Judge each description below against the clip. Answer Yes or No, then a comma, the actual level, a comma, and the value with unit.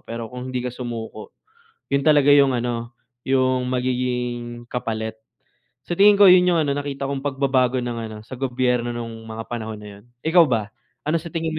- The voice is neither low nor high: No, low, 125 Hz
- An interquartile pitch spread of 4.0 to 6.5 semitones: No, average, 3.0 semitones